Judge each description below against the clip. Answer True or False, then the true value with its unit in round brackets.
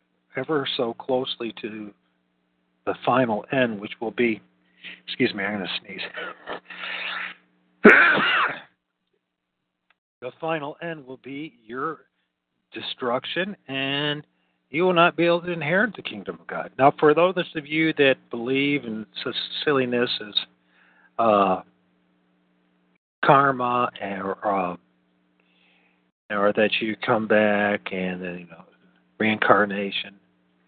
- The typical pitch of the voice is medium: False (105 Hz)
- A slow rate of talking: True (115 wpm)